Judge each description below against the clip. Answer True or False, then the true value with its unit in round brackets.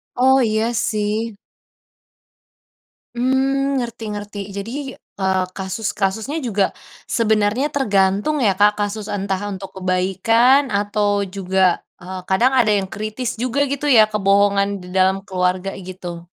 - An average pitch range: True (3.2 semitones)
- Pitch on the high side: True (205 Hz)